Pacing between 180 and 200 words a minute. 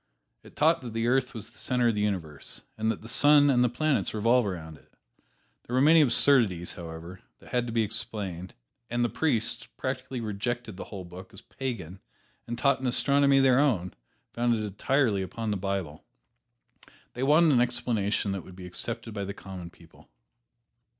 Yes: average, 185 wpm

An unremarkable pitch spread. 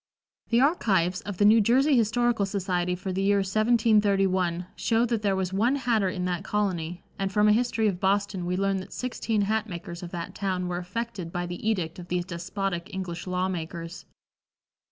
Yes: average, 3.2 semitones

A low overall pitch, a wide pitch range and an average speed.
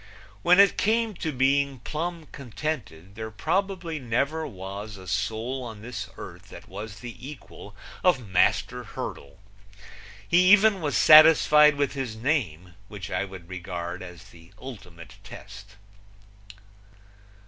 No: low, 120 Hz; wide, 7.8 semitones; slow, 130 wpm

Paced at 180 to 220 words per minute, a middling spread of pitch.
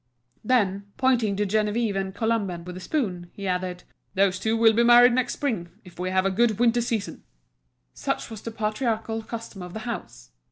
Yes: average, 190 wpm; average, 3.7 semitones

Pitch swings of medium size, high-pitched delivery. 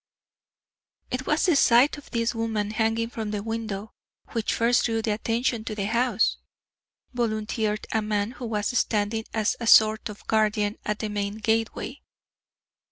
No: narrow, 1.6 semitones; high, 220 Hz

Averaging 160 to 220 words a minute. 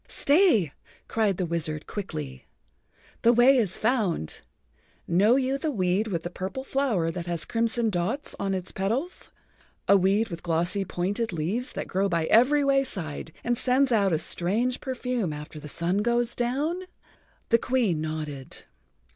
No: average, 150 wpm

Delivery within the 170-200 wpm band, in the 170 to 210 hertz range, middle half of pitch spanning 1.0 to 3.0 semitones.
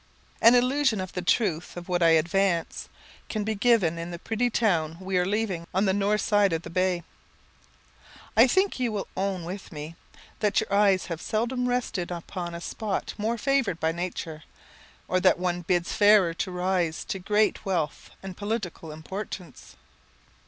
No: average, 175 wpm; high, 190 Hz; average, 3.8 semitones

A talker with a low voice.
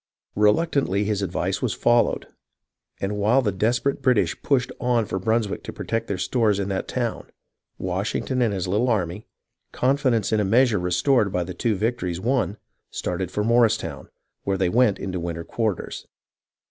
Yes: low, 105 Hz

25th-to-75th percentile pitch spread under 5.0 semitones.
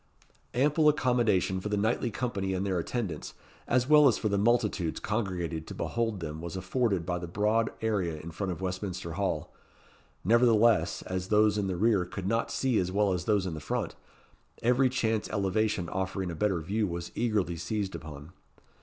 Yes: average, 4.0 semitones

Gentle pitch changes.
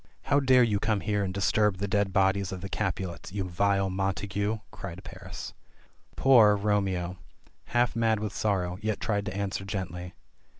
Yes: narrow, 1.8 semitones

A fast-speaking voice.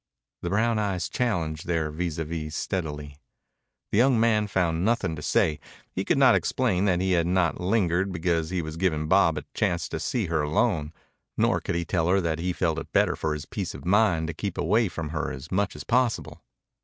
Yes: fast, 215 wpm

